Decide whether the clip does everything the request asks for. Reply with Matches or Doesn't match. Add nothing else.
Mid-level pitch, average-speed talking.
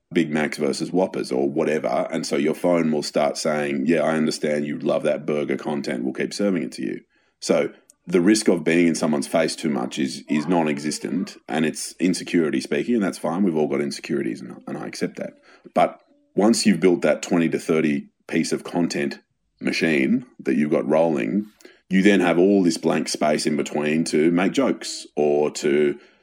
Doesn't match